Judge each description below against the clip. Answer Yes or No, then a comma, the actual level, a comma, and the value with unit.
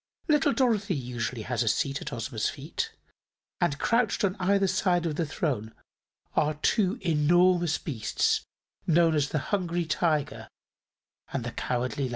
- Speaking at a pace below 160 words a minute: Yes, average, 145 wpm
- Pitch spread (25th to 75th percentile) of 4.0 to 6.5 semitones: Yes, average, 5.3 semitones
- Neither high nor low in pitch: Yes, medium, 160 Hz